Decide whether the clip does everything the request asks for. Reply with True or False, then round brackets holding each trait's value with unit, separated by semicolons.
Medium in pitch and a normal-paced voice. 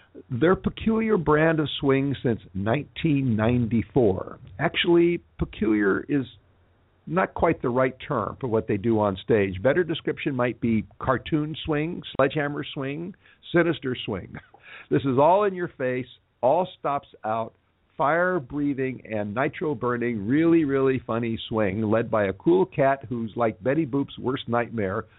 False (130 Hz; 145 wpm)